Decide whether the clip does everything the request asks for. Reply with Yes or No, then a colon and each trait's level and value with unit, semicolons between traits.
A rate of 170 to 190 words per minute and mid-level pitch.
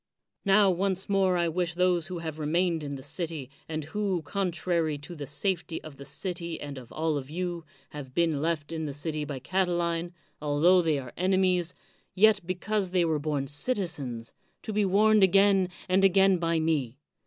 Yes: average, 185 wpm; medium, 170 Hz